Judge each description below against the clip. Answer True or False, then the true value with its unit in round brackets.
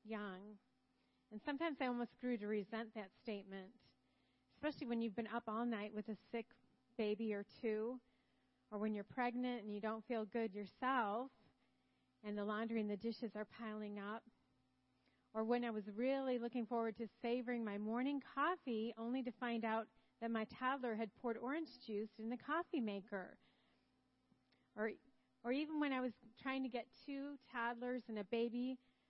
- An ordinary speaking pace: True (170 wpm)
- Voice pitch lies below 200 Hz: False (230 Hz)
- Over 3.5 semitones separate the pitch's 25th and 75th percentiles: False (2.8 semitones)